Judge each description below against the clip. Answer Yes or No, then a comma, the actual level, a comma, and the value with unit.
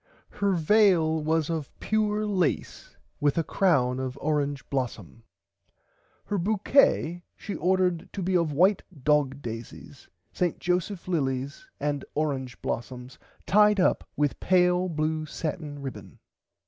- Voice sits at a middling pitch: Yes, medium, 160 Hz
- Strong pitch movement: No, average, 4.7 semitones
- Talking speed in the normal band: No, slow, 125 wpm